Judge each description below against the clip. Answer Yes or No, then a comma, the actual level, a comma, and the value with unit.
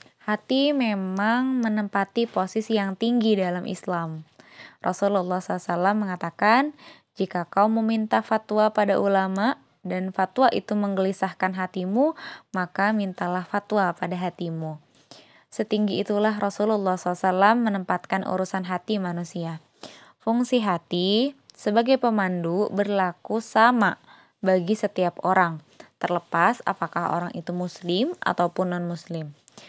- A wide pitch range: No, average, 3.1 semitones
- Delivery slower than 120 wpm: Yes, average, 105 wpm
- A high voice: Yes, high, 195 Hz